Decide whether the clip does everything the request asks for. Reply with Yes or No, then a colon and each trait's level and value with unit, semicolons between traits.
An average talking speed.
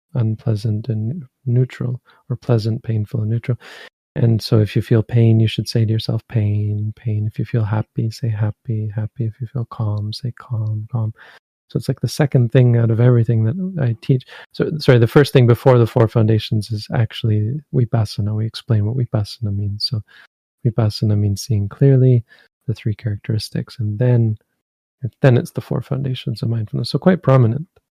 Yes: average, 180 wpm